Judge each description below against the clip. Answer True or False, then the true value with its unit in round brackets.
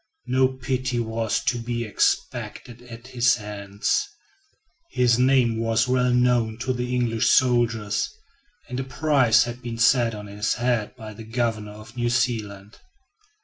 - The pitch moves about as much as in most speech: False (2.0 semitones)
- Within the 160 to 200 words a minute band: False (145 wpm)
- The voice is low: True (120 Hz)